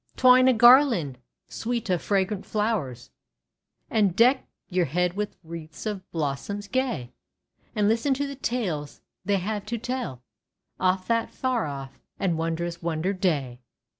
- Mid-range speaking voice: No, high, 195 Hz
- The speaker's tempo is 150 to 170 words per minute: No, average, 140 wpm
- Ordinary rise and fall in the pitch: No, wide, 6.0 semitones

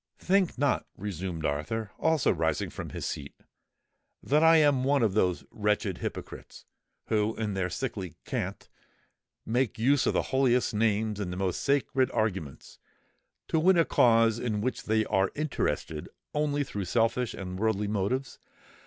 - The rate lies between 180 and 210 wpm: No, average, 155 wpm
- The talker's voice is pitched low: Yes, low, 110 Hz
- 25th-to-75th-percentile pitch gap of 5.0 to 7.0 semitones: Yes, wide, 5.4 semitones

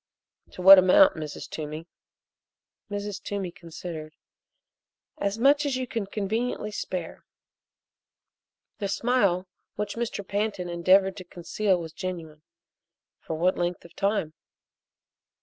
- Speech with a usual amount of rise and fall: Yes, average, 3.4 semitones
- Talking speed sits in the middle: No, slow, 115 wpm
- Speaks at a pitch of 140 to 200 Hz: Yes, high, 190 Hz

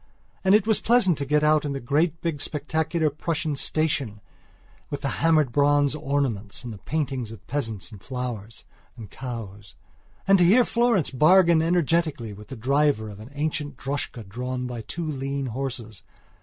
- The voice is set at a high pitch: No, medium, 140 Hz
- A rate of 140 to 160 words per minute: No, average, 170 wpm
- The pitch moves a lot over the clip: No, average, 4.9 semitones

